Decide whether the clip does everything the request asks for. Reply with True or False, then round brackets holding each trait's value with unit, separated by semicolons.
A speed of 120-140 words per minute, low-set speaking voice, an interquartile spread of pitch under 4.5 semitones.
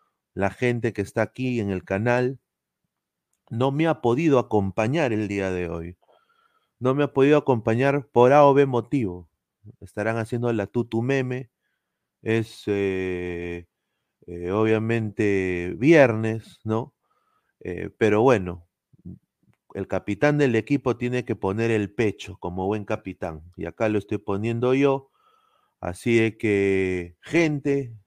False (135 wpm; 110 Hz; 4.8 semitones)